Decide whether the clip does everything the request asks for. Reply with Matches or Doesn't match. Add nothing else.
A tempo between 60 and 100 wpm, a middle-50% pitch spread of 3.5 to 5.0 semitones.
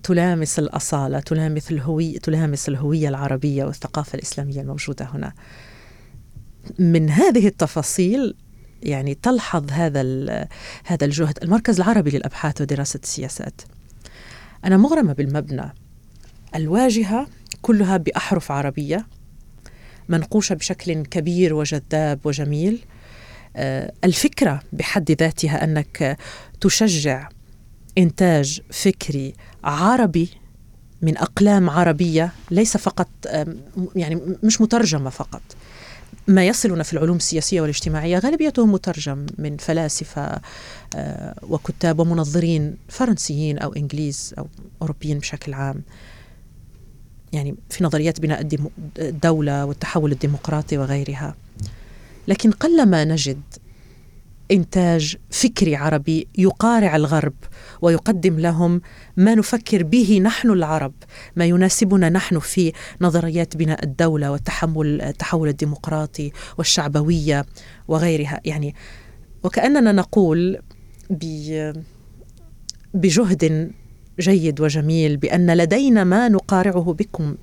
Matches